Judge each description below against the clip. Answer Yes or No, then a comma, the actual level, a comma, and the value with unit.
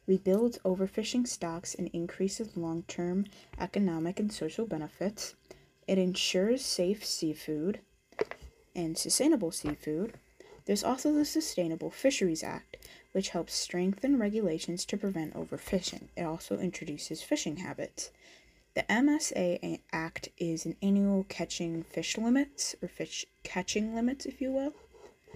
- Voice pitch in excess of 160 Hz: Yes, high, 190 Hz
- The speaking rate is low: Yes, slow, 120 wpm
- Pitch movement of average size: No, wide, 5.9 semitones